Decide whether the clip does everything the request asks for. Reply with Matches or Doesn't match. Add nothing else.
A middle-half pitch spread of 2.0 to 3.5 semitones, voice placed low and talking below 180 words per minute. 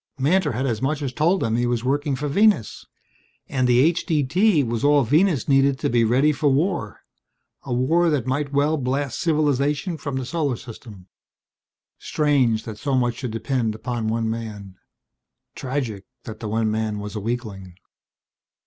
Doesn't match